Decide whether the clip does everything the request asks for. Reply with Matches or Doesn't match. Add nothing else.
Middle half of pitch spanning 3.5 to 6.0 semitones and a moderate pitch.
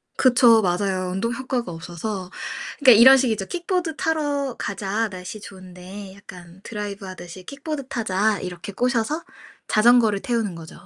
Doesn't match